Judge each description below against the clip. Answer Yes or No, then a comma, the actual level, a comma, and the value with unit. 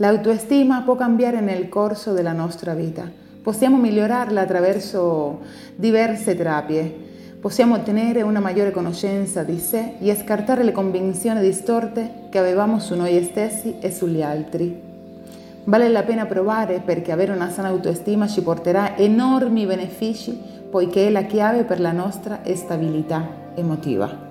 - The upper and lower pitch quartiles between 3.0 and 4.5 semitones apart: Yes, average, 4.1 semitones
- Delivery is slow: No, average, 145 wpm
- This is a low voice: No, high, 200 Hz